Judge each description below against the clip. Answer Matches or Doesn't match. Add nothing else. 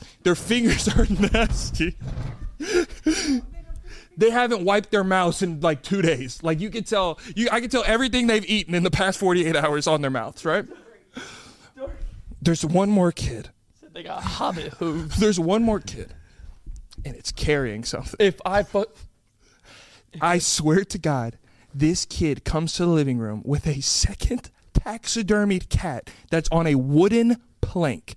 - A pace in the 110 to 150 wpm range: Matches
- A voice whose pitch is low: Doesn't match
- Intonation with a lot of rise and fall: Matches